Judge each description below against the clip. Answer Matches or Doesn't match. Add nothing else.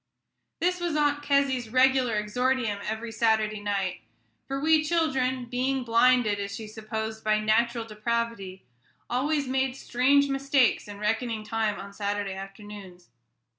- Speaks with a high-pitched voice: Matches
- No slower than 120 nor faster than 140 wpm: Matches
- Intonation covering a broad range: Doesn't match